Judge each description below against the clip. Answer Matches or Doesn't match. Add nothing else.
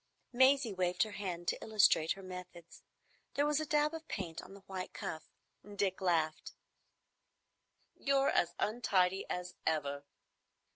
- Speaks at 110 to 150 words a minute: Matches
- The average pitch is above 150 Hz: Matches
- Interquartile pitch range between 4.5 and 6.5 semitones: Matches